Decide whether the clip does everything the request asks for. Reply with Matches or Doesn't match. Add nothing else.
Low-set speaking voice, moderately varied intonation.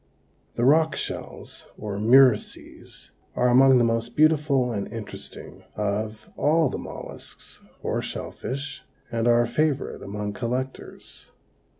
Matches